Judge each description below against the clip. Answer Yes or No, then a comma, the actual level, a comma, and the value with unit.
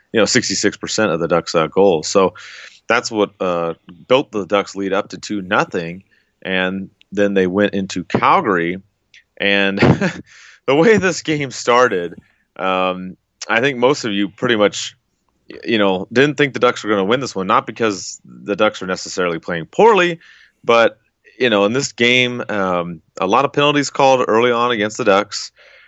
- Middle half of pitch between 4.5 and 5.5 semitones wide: Yes, average, 5.0 semitones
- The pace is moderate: Yes, average, 180 wpm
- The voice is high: No, low, 105 Hz